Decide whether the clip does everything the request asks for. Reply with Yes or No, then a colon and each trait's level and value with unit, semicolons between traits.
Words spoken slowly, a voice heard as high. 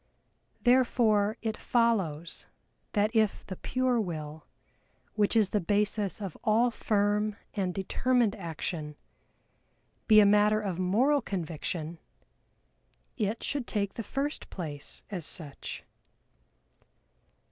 Yes: slow, 110 wpm; high, 205 Hz